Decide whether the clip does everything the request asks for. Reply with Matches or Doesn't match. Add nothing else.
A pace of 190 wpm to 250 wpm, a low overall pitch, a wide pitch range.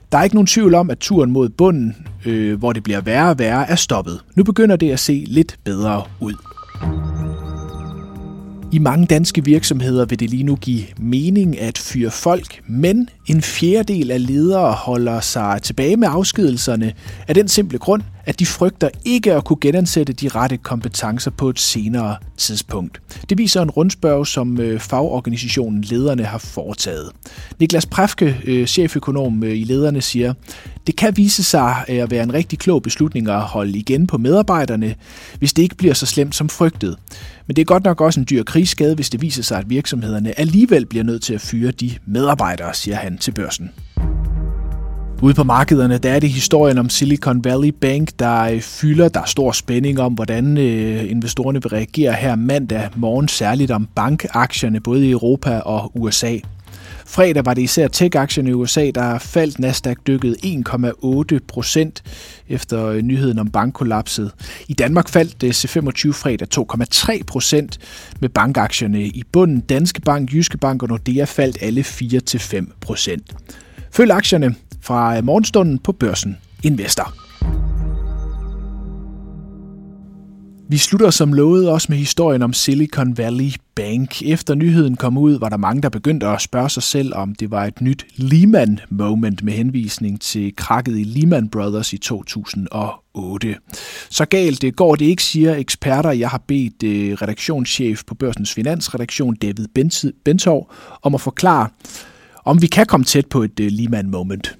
Doesn't match